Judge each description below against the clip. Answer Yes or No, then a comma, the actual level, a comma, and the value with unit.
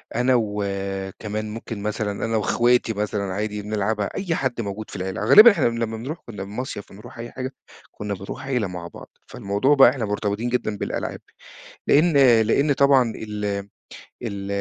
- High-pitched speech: No, low, 110 Hz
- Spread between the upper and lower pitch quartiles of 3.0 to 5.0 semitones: Yes, average, 3.4 semitones